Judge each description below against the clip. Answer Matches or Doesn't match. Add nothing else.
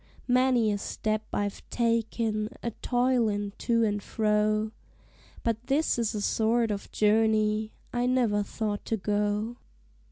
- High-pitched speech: Matches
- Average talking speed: Doesn't match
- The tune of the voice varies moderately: Doesn't match